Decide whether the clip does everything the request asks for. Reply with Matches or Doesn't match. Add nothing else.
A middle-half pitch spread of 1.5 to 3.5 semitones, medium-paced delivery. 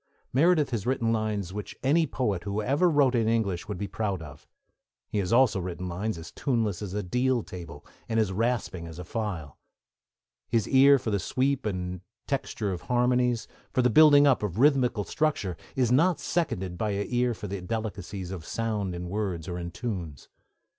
Doesn't match